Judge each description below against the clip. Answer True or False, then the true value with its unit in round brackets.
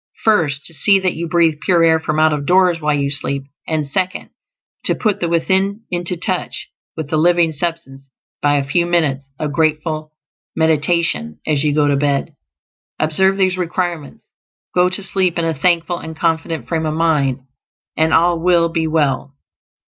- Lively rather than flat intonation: False (2.8 semitones)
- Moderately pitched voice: True (160 Hz)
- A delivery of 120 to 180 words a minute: True (175 wpm)